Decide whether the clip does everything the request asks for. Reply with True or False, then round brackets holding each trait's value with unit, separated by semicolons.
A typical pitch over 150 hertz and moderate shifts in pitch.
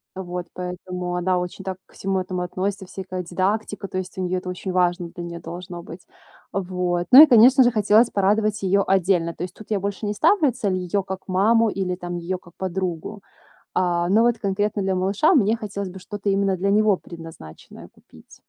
False (190 Hz; 2.3 semitones)